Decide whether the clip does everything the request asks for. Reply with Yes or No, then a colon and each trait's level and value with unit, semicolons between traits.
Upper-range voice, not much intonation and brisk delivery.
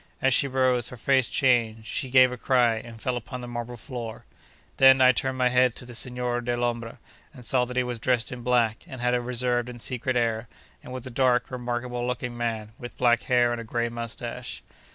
No: low, 125 Hz; narrow, 1.1 semitones; fast, 215 wpm